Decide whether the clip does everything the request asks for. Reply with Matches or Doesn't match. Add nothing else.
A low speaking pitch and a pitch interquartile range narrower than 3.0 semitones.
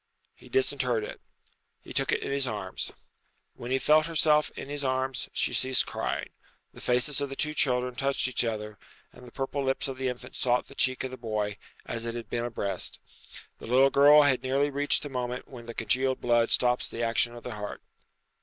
Matches